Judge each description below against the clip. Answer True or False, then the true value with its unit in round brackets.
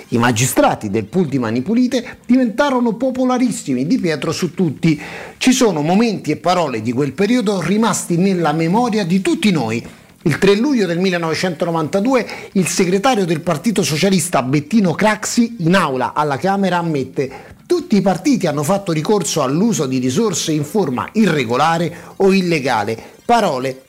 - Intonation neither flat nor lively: False (6.2 semitones)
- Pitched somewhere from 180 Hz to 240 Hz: True (185 Hz)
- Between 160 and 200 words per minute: False (145 wpm)